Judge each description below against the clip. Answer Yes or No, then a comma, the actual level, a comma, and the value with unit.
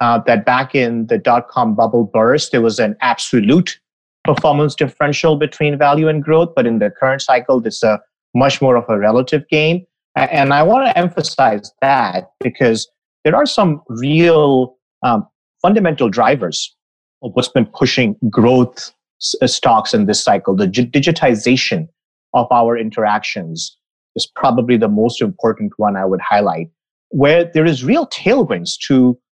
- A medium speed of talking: Yes, average, 150 wpm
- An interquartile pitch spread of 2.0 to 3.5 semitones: No, average, 5.3 semitones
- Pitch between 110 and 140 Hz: Yes, low, 135 Hz